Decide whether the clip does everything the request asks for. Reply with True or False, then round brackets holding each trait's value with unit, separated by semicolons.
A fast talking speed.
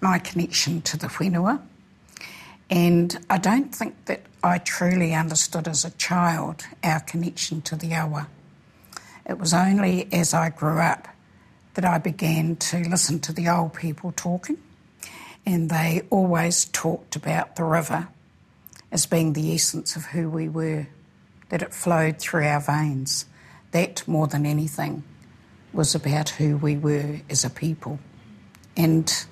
False (145 wpm)